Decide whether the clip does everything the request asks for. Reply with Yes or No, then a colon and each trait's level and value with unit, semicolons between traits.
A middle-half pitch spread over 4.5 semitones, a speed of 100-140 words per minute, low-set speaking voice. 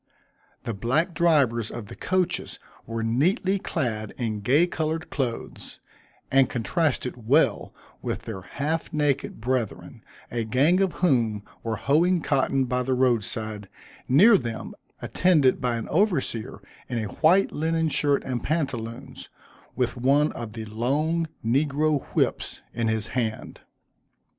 Yes: wide, 5.5 semitones; slow, 135 wpm; low, 130 Hz